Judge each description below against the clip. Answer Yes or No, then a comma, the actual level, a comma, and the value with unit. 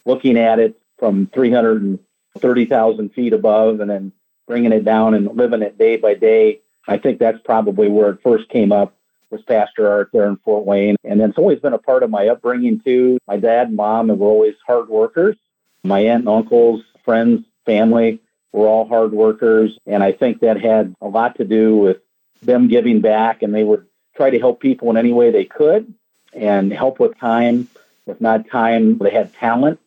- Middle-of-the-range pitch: No, low, 115 Hz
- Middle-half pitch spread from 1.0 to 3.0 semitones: Yes, narrow, 2.4 semitones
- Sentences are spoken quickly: No, average, 195 wpm